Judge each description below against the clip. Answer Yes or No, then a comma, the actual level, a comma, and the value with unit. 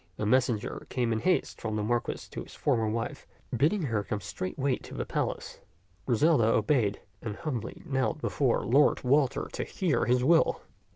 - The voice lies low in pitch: Yes, low, 125 Hz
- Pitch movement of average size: Yes, average, 4.5 semitones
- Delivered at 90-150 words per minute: No, average, 170 wpm